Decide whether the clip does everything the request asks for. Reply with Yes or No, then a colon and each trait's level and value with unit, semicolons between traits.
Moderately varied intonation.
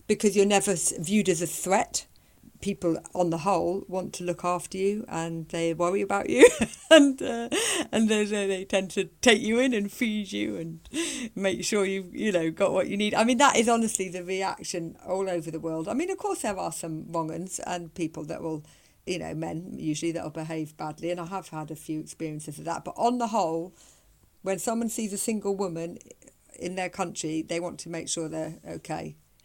Yes: average, 4.2 semitones